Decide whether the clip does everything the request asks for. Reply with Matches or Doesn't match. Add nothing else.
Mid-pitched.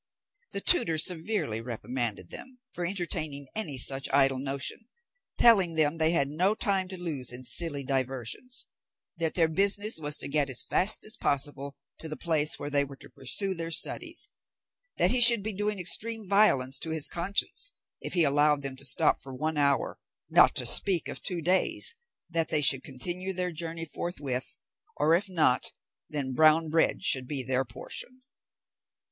Matches